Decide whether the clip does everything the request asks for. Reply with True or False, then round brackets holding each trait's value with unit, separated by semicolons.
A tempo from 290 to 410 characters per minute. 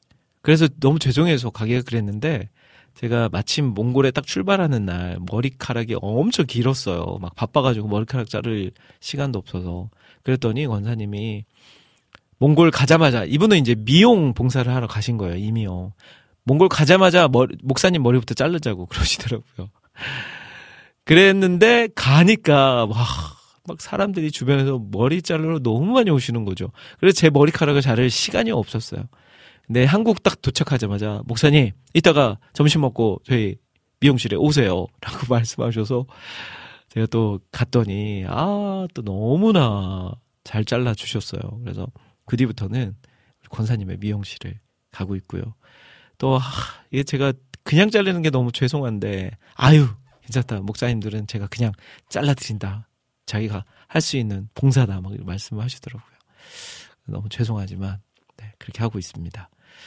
True (320 characters per minute)